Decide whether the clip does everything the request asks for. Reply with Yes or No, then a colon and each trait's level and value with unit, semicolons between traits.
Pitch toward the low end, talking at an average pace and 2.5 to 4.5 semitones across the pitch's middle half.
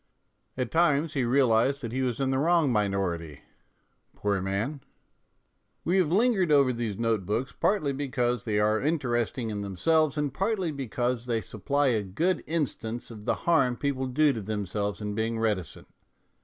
No: low, 125 Hz; average, 165 wpm; average, 5.2 semitones